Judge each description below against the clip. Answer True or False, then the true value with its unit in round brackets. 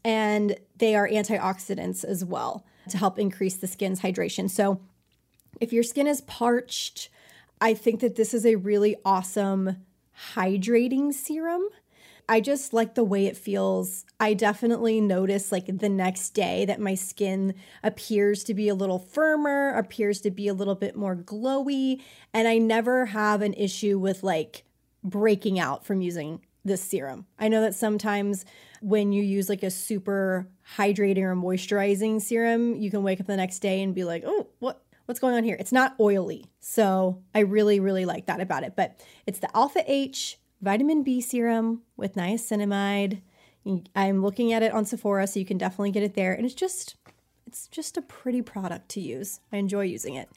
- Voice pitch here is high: True (205 Hz)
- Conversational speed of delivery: True (180 wpm)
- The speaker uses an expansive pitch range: False (2.9 semitones)